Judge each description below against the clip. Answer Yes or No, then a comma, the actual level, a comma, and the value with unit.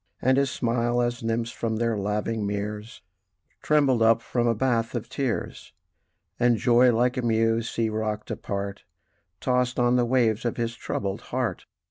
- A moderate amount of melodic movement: No, narrow, 1.7 semitones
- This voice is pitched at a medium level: No, low, 115 Hz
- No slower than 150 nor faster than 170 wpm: Yes, average, 160 wpm